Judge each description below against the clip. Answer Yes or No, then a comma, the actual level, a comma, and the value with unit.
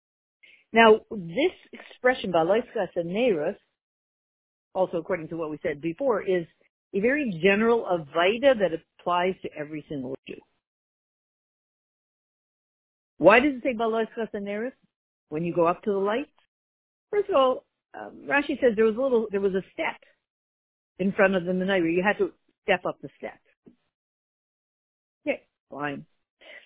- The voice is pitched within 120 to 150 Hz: No, high, 195 Hz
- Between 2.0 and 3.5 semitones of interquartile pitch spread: No, average, 5.2 semitones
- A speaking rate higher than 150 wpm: No, average, 145 wpm